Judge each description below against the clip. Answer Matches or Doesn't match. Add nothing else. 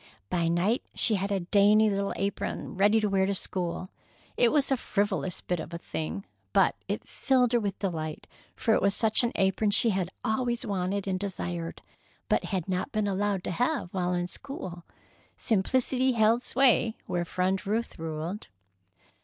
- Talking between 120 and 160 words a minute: Doesn't match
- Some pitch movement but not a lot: Matches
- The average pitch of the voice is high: Matches